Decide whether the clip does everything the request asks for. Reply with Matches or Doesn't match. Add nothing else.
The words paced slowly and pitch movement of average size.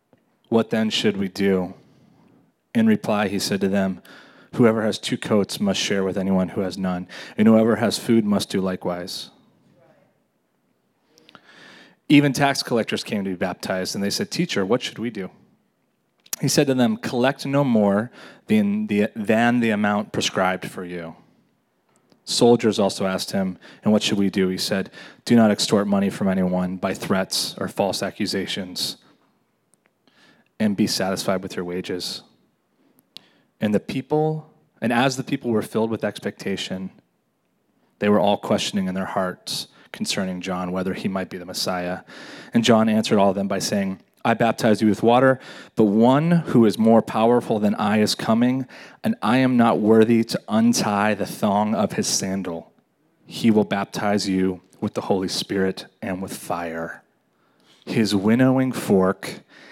Doesn't match